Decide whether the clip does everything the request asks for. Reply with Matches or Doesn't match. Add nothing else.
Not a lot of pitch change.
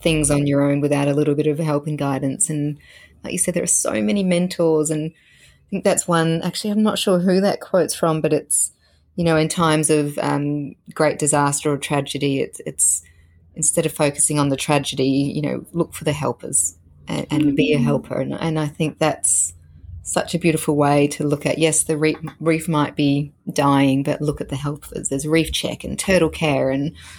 Matches